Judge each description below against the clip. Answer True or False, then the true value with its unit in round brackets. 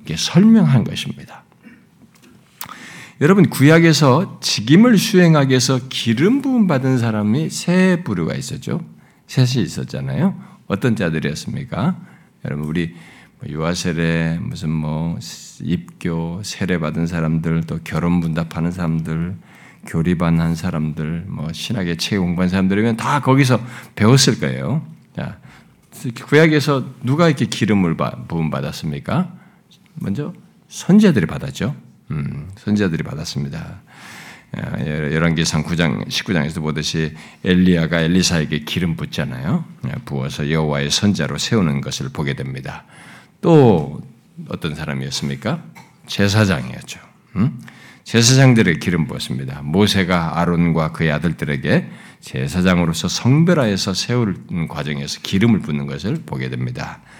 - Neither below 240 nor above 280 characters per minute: False (290 characters per minute)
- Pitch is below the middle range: True (90 Hz)